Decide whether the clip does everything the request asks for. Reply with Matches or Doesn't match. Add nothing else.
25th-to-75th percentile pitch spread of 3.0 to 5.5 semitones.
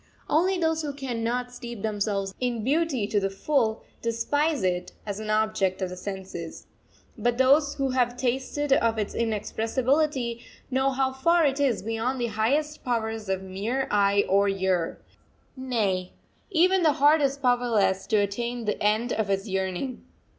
Matches